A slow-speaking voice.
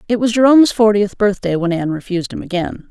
No: fast, 205 wpm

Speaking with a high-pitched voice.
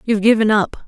Yes: high, 215 Hz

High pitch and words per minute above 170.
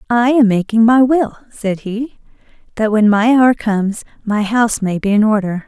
Yes: high, 220 Hz; average, 190 wpm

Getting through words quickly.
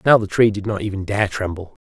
Yes: fast, 265 wpm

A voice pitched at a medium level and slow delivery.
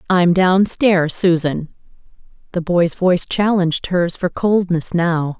Yes: medium, 175 Hz; slow, 120 wpm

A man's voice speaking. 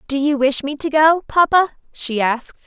No: female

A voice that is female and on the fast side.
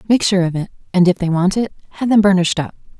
Yes: female; fast, 260 wpm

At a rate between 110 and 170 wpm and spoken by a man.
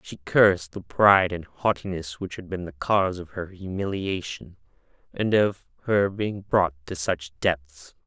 Yes: average, 165 wpm; male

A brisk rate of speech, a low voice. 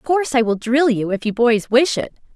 No: fast, 280 wpm; very high, 250 Hz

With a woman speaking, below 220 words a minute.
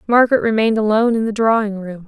Yes: female; average, 200 wpm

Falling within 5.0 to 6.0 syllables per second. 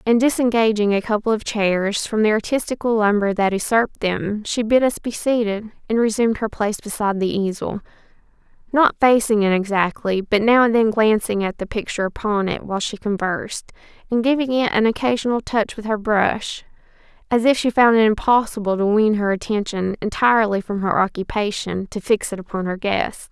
Yes: 5.4 syllables/s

